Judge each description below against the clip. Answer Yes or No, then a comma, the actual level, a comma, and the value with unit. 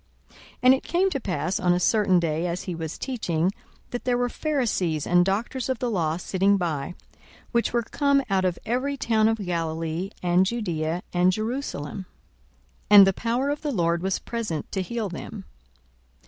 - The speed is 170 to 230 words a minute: Yes, average, 180 wpm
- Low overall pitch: No, high, 195 Hz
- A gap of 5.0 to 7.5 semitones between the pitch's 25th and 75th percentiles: Yes, wide, 5.5 semitones